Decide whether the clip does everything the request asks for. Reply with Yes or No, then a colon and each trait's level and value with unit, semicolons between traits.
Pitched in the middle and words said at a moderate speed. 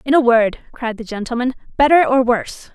No: high, 245 Hz; average, 195 wpm